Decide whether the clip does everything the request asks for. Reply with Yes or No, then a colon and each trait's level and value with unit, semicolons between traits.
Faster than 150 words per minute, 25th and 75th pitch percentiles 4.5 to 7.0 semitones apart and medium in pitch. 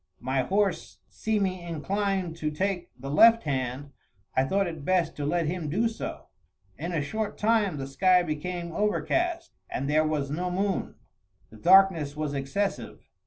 Yes: average, 160 wpm; average, 5.1 semitones; medium, 175 Hz